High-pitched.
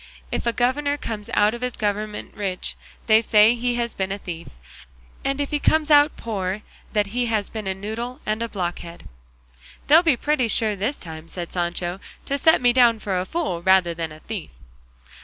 Yes: high, 215 Hz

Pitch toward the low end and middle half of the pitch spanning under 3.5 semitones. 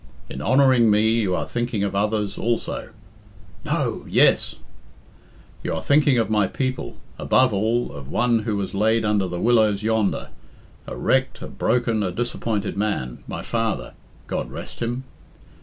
Yes: low, 110 Hz; average, 2.9 semitones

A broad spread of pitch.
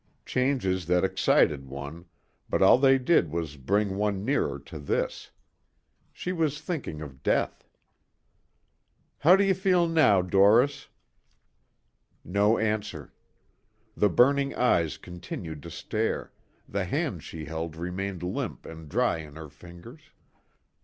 Yes: wide, 8.3 semitones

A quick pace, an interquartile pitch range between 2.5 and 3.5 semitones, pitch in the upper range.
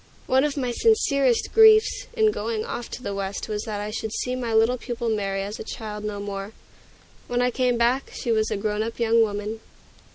Yes: fast, 215 wpm; average, 3.1 semitones; high, 225 Hz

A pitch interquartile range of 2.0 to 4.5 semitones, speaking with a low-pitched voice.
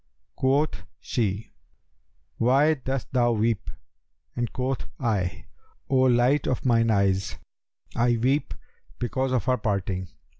Yes: average, 3.3 semitones; low, 120 Hz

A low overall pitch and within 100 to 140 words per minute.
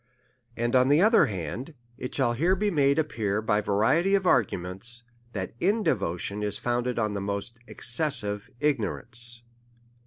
No: low, 120 Hz; average, 155 wpm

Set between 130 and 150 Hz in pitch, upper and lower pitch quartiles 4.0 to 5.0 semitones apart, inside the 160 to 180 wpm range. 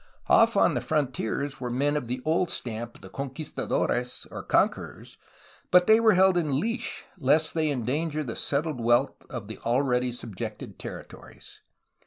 Yes: medium, 140 Hz; average, 4.4 semitones; average, 165 wpm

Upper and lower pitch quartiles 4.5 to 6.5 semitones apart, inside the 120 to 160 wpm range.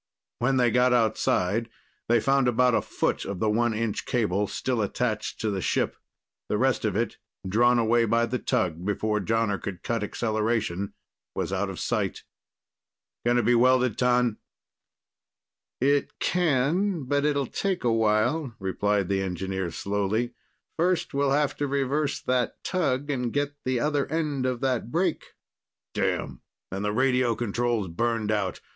No: average, 3.9 semitones; average, 155 wpm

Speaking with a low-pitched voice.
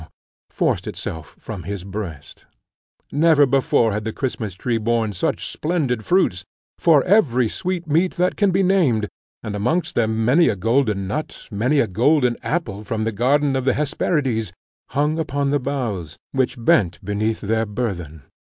Yes: low, 120 Hz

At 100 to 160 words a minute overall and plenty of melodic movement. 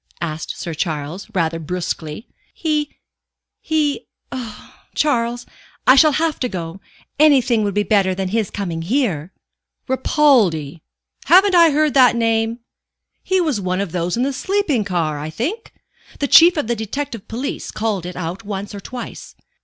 Yes: average, 155 wpm; wide, 7.7 semitones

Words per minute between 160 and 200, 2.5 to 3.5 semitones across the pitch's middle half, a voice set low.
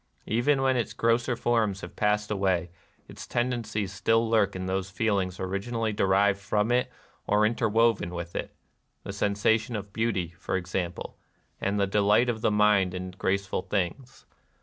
Yes: average, 170 wpm; average, 3.0 semitones; low, 105 Hz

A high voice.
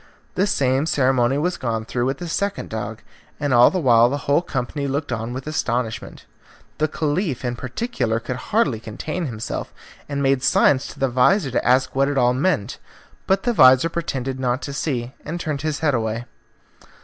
No: low, 135 Hz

